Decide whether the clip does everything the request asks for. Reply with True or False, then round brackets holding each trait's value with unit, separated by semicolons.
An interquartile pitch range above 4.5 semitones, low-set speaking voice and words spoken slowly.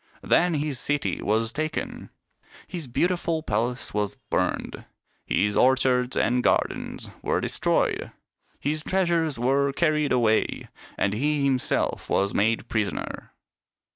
True (5.2 semitones; 130 Hz; 120 wpm)